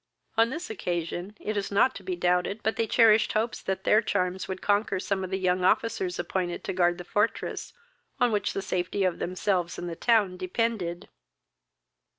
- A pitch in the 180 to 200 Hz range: Yes, high, 190 Hz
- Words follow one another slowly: No, average, 185 wpm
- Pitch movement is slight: No, average, 3.1 semitones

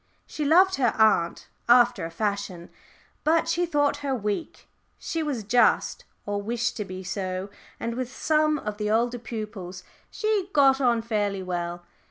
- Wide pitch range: Yes, wide, 5.9 semitones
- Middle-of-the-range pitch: No, high, 230 Hz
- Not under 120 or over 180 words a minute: Yes, average, 160 wpm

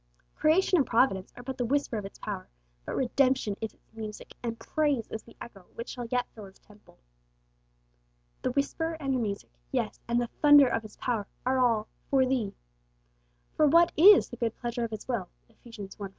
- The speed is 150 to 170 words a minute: No, average, 200 wpm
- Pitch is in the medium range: No, high, 240 Hz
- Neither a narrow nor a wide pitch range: Yes, average, 3.7 semitones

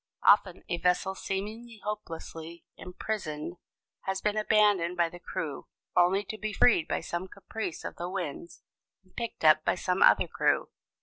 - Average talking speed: Yes, average, 160 wpm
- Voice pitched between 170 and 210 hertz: Yes, medium, 185 Hz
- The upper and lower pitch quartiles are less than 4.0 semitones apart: Yes, average, 3.5 semitones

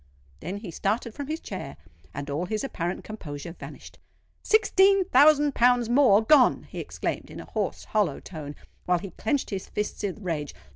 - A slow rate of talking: No, average, 175 wpm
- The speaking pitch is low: No, high, 210 Hz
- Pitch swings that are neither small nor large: No, wide, 8.0 semitones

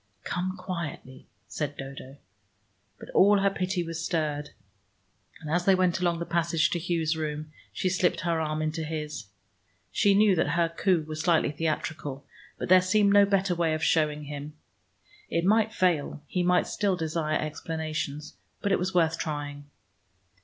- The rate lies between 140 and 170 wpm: Yes, average, 165 wpm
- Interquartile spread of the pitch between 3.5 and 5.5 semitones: No, average, 3.0 semitones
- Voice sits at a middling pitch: Yes, medium, 165 Hz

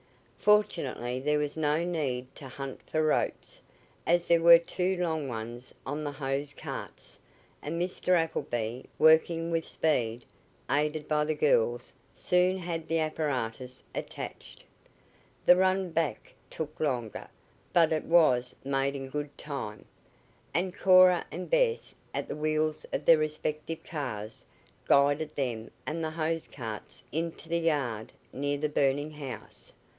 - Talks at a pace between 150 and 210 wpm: No, average, 140 wpm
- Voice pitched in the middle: Yes, medium, 150 Hz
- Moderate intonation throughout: Yes, average, 3.5 semitones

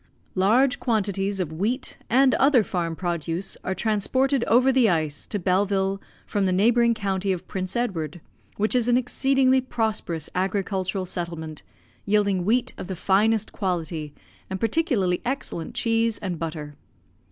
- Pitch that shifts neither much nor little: Yes, average, 4.6 semitones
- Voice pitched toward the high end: Yes, high, 195 Hz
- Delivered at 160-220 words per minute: No, average, 140 wpm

